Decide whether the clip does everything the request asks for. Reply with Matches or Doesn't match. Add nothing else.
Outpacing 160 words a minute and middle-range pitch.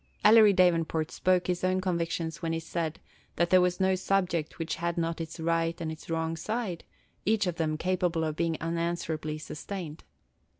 Matches